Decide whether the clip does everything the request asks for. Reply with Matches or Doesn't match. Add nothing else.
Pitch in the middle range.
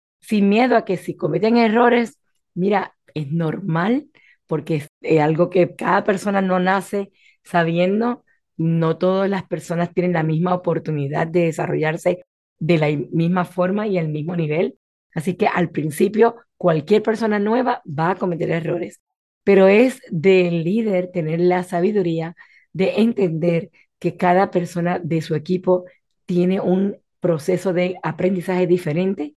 Matches